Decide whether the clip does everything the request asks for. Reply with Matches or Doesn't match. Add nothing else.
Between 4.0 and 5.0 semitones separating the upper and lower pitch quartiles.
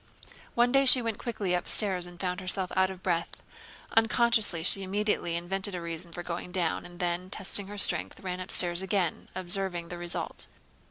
Doesn't match